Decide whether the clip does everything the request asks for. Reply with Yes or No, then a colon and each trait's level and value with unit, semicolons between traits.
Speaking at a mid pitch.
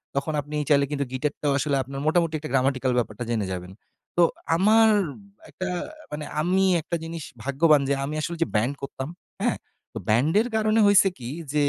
Yes: medium, 150 Hz